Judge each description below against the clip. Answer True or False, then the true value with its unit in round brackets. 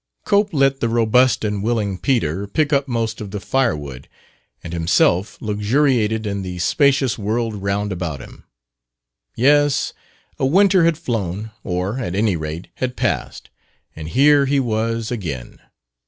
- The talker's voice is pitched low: True (110 Hz)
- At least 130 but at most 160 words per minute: True (145 wpm)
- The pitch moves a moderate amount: False (5.7 semitones)